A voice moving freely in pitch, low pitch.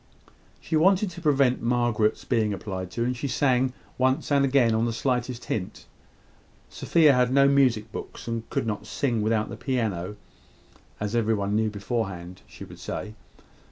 No: average, 3.6 semitones; low, 120 Hz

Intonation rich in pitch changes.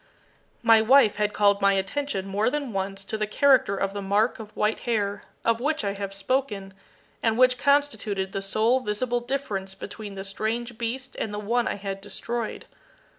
No: average, 3.5 semitones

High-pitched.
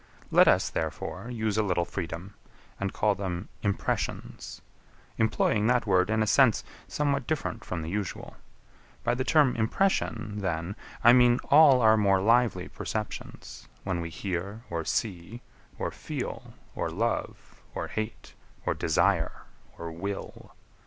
No: low, 105 Hz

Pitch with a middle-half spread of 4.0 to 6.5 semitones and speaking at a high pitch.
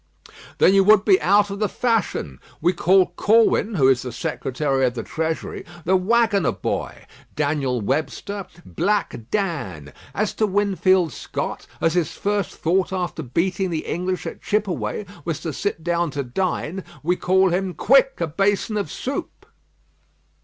No: average, 4.5 semitones; medium, 180 Hz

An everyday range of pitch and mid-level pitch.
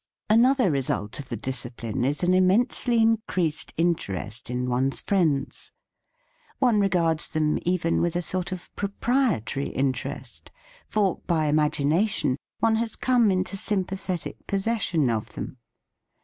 No: wide, 6.8 semitones; medium, 175 Hz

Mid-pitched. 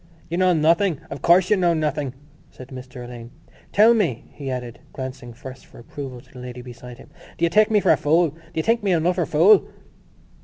Yes: medium, 150 Hz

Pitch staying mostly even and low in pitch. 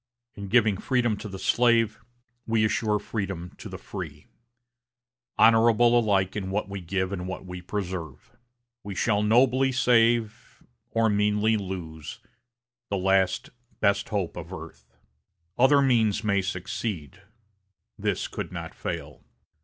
No: average, 3.3 semitones; low, 105 Hz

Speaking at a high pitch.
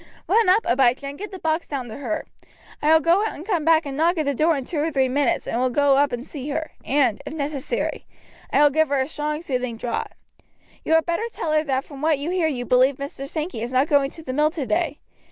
Yes: very high, 290 Hz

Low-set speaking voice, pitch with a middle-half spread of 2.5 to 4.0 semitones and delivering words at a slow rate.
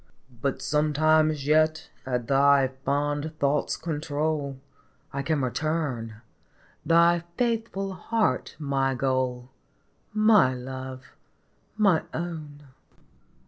No: medium, 145 Hz; average, 3.1 semitones; slow, 90 wpm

